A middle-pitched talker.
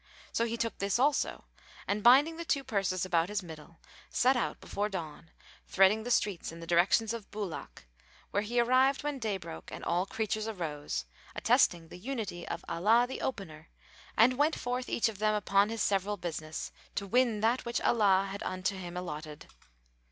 No: high, 205 Hz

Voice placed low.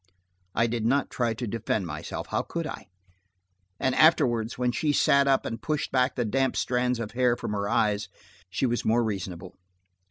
Yes: low, 120 Hz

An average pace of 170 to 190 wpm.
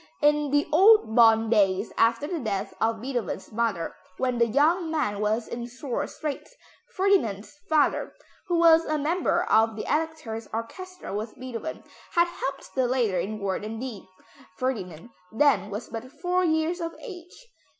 No: average, 160 wpm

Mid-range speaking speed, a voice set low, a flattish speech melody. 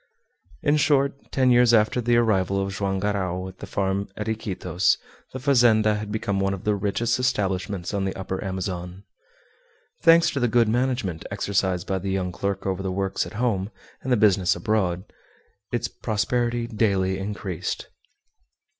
No: average, 165 wpm; low, 100 Hz; average, 3.7 semitones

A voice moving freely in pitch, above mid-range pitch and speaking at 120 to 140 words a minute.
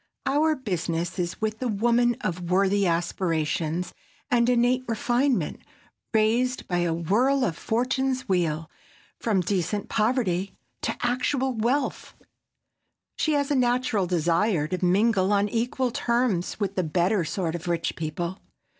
Yes: wide, 5.9 semitones; high, 205 Hz; slow, 135 wpm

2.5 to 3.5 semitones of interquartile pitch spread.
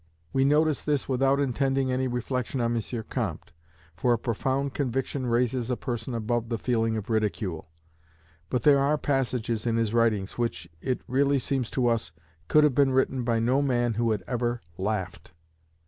Yes: average, 2.8 semitones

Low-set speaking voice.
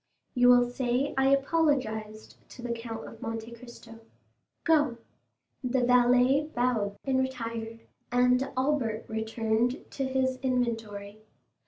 No: high, 245 Hz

